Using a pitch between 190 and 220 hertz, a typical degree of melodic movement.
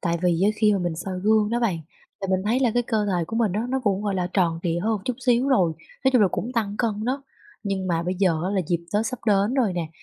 Yes: high, 205 Hz; average, 4.0 semitones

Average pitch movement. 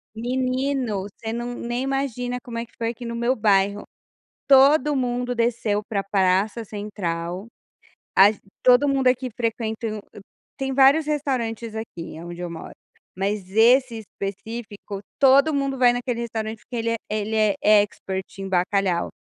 Yes: average, 3.7 semitones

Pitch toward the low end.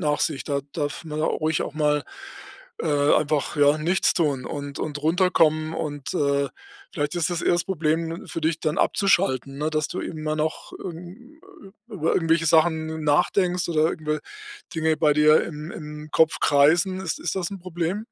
No: medium, 155 Hz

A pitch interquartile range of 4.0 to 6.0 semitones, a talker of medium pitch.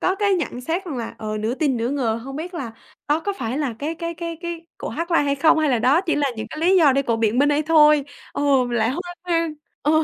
No: average, 4.9 semitones; very high, 295 Hz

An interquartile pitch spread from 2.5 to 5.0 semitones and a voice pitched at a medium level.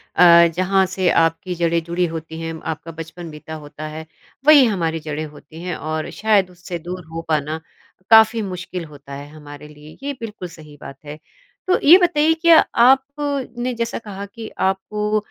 No: wide, 5.6 semitones; medium, 180 Hz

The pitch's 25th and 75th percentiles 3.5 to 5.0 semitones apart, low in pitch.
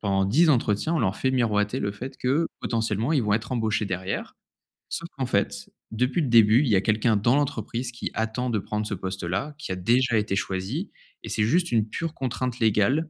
Yes: average, 4.1 semitones; low, 115 Hz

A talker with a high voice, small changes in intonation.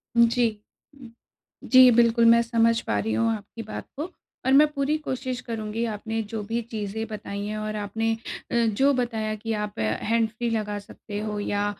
Yes: high, 225 Hz; narrow, 1.8 semitones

